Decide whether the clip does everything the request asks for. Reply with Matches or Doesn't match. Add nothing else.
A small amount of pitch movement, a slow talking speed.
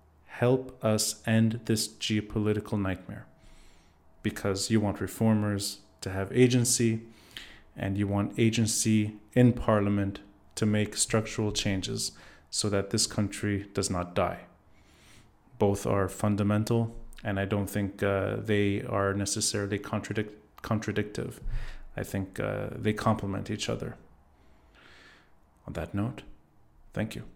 Matches